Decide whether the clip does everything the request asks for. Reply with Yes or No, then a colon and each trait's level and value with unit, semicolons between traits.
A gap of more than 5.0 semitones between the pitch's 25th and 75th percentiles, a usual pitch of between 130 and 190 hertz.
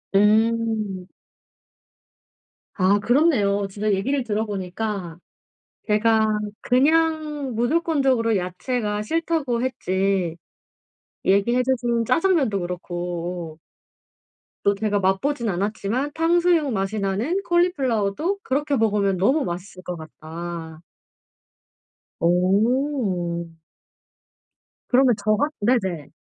No: wide, 5.6 semitones; high, 215 Hz